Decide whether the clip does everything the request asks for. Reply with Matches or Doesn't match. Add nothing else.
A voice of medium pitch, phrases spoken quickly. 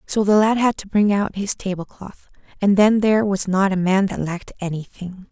Doesn't match